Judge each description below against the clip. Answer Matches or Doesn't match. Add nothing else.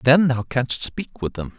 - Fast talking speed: Matches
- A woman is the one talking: Doesn't match